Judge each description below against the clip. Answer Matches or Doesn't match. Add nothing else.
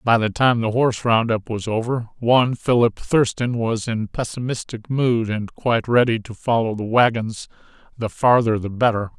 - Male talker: Matches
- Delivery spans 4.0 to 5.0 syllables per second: Matches